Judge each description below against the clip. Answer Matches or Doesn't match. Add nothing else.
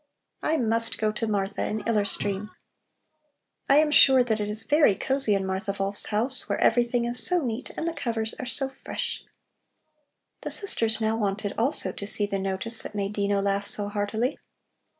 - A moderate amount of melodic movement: Matches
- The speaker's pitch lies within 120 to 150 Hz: Doesn't match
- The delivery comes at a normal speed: Matches